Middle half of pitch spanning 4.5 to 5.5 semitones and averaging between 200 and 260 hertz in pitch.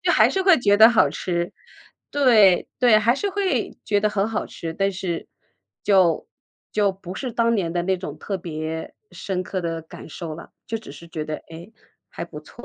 No: average, 4.8 semitones; high, 190 Hz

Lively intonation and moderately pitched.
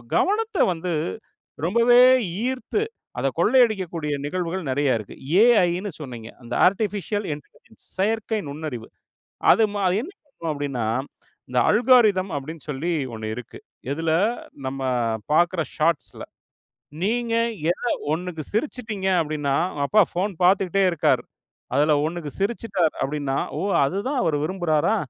Yes: wide, 6.4 semitones; medium, 175 Hz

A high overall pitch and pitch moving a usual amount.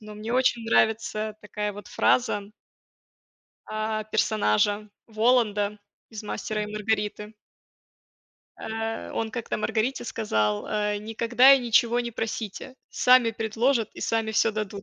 No: high, 220 Hz; narrow, 1.5 semitones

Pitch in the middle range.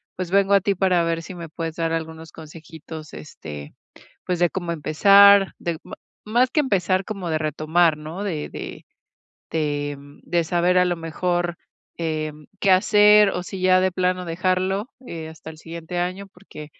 Yes: medium, 175 Hz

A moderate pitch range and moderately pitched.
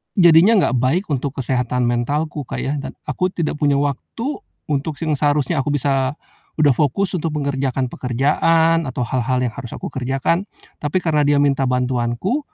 Yes: average, 3.7 semitones; medium, 145 Hz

